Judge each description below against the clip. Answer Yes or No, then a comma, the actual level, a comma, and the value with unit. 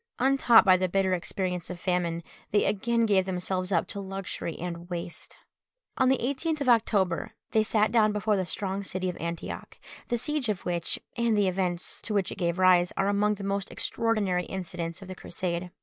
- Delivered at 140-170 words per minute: No, average, 195 wpm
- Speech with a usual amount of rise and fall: Yes, average, 3.2 semitones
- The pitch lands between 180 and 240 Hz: Yes, high, 190 Hz